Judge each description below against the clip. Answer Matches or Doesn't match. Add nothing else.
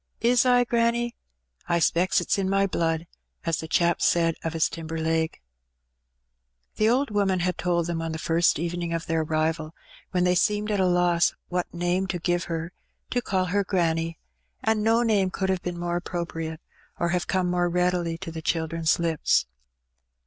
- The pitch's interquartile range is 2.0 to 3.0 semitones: Matches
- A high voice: Doesn't match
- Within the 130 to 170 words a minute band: Doesn't match